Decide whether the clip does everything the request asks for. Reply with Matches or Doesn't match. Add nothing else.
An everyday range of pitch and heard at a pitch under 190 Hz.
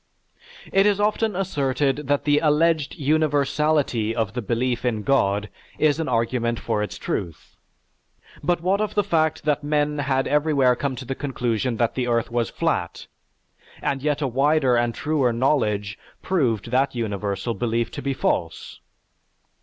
Matches